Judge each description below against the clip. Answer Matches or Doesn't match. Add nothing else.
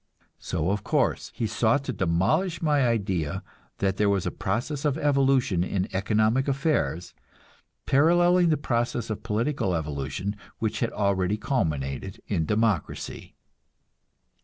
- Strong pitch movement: Matches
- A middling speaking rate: Doesn't match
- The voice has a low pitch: Matches